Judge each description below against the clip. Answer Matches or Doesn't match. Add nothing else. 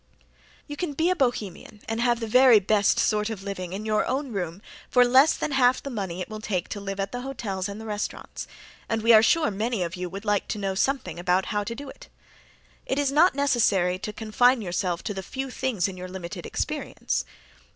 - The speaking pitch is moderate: Doesn't match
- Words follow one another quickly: Matches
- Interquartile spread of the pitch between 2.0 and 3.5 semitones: Doesn't match